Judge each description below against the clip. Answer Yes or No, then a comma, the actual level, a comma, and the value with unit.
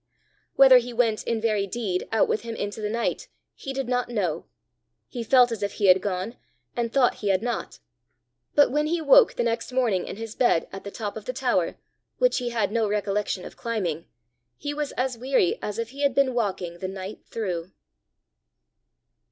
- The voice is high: Yes, high, 230 Hz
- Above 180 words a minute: Yes, average, 200 wpm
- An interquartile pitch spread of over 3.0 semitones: Yes, average, 3.7 semitones